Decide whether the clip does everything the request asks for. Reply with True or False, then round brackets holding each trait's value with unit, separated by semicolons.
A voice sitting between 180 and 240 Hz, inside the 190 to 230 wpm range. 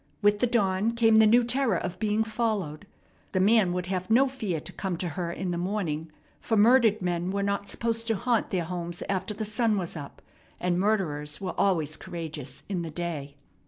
True (190 Hz; 200 wpm)